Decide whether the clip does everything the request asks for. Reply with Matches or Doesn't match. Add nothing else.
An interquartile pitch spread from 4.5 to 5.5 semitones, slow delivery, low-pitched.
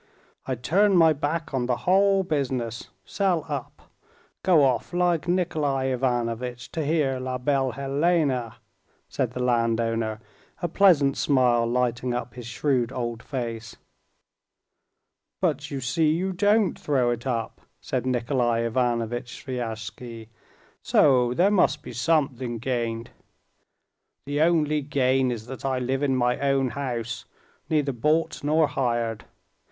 Doesn't match